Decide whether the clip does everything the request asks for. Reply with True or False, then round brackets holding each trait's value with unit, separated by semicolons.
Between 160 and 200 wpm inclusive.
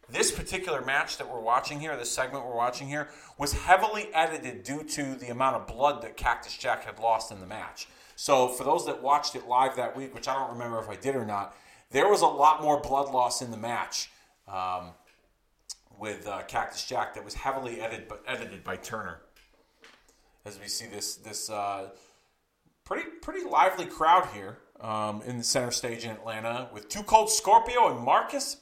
True (195 wpm)